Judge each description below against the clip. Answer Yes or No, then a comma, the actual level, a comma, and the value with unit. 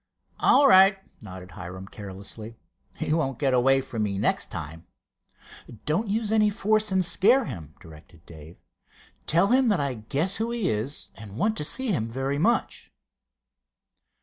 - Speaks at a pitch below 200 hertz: Yes, low, 135 Hz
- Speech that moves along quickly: No, average, 155 wpm